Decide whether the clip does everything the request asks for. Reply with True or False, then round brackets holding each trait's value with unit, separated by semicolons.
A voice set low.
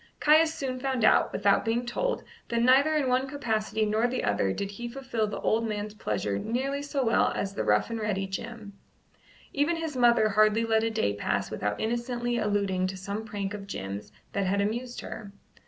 False (225 Hz)